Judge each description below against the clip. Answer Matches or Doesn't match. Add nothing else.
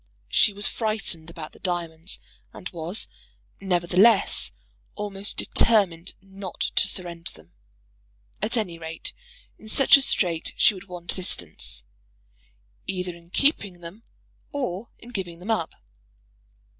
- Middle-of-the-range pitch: Matches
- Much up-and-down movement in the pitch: Doesn't match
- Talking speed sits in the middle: Doesn't match